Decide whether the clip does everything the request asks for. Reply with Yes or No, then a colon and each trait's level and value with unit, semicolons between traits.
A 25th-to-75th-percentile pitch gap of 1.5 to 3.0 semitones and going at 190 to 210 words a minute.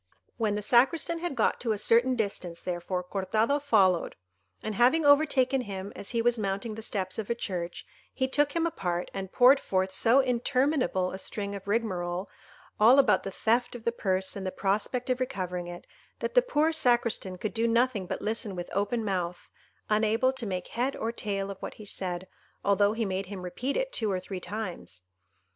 No: average, 4.8 semitones; average, 195 wpm